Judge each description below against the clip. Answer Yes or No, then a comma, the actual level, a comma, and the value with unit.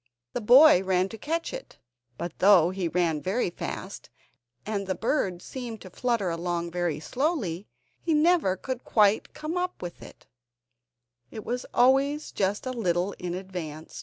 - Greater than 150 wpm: Yes, average, 160 wpm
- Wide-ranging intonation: Yes, wide, 6.4 semitones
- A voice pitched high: Yes, high, 200 Hz